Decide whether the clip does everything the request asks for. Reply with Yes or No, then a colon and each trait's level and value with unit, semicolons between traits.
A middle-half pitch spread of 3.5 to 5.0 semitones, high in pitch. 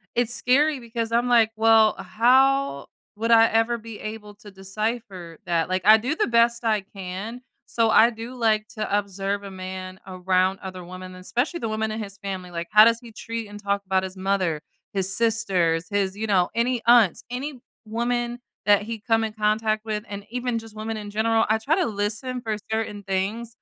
No: average, 3.1 semitones; high, 215 Hz